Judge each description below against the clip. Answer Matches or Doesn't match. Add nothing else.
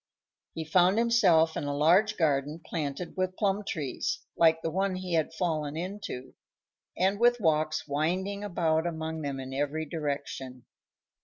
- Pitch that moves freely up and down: Doesn't match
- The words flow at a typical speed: Matches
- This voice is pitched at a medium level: Matches